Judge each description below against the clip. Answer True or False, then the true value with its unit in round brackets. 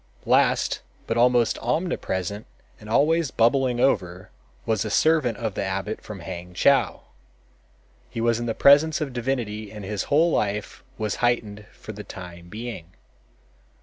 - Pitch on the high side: False (110 Hz)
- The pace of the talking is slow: False (145 wpm)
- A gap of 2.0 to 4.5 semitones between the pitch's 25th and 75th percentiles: True (3.8 semitones)